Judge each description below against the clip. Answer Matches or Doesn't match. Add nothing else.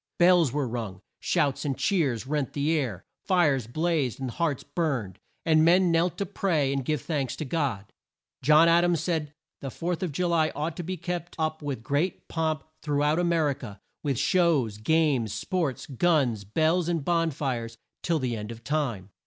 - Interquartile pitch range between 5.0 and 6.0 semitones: Doesn't match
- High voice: Doesn't match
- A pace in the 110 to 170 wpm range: Doesn't match